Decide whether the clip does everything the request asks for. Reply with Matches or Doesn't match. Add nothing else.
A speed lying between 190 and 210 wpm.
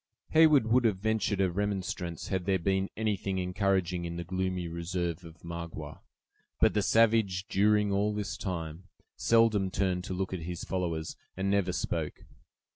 Doesn't match